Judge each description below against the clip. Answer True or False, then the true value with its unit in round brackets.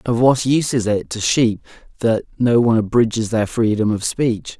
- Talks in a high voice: False (115 Hz)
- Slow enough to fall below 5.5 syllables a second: True (5.0 syllables/s)